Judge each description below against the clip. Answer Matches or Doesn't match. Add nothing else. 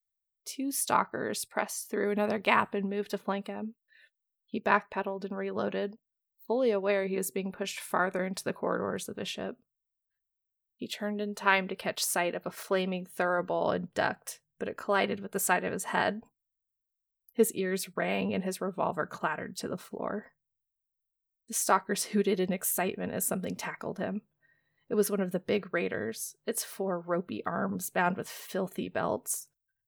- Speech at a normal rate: Matches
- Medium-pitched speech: Doesn't match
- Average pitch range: Doesn't match